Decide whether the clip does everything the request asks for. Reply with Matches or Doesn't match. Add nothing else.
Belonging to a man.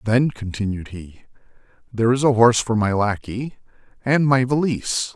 Matches